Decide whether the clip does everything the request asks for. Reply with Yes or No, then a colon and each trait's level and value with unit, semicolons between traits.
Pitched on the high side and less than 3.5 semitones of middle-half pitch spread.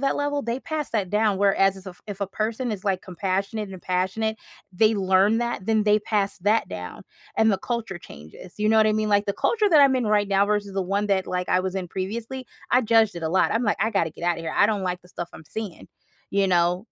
Yes: high, 205 Hz; average, 2.9 semitones